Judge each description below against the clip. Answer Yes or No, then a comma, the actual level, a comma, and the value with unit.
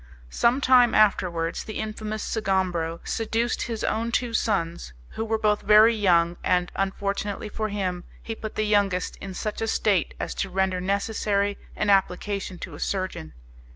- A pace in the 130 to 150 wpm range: No, average, 160 wpm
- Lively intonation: No, average, 2.9 semitones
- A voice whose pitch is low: No, high, 200 Hz